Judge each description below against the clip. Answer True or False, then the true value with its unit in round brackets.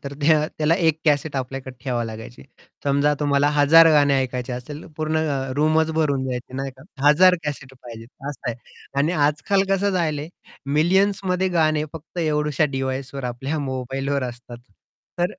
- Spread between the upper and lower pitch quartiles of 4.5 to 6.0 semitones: False (3.1 semitones)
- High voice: False (145 Hz)